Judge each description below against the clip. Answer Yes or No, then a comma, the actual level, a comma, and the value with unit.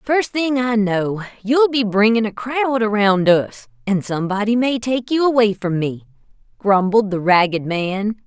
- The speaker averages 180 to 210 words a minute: No, average, 165 wpm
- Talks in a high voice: Yes, high, 215 Hz